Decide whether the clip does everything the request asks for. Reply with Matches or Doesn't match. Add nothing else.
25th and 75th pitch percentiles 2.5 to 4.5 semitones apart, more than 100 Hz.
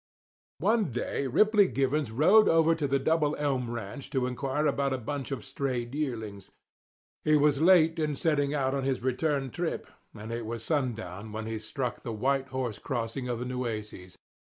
Matches